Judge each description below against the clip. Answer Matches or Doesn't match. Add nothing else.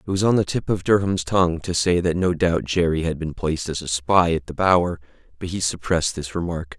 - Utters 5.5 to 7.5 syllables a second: Matches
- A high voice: Doesn't match